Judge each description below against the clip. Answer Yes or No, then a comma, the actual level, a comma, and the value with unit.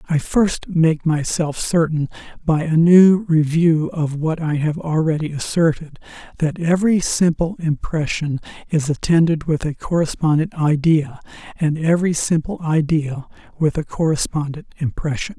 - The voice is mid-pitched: Yes, medium, 160 Hz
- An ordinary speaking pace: No, slow, 130 wpm